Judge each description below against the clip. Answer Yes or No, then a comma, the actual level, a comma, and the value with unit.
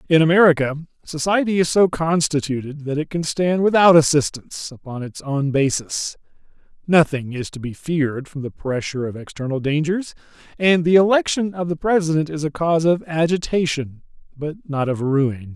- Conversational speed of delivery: Yes, average, 160 wpm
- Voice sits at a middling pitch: Yes, medium, 155 Hz